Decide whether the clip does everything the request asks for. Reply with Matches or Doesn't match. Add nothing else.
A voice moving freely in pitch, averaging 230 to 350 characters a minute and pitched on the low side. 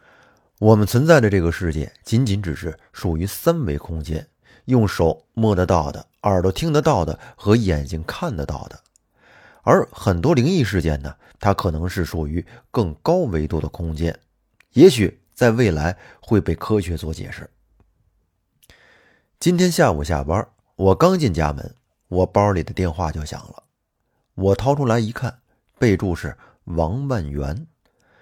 Doesn't match